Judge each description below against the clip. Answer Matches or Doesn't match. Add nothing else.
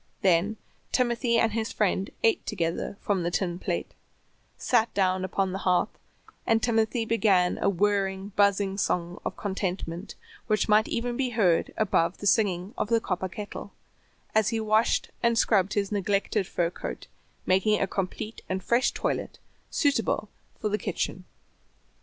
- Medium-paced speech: Matches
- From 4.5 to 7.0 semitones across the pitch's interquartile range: Doesn't match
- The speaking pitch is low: Doesn't match